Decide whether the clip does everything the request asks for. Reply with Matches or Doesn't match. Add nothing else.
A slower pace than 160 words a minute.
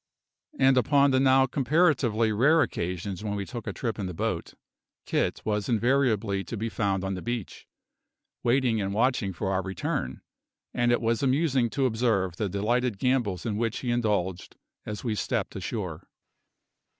Doesn't match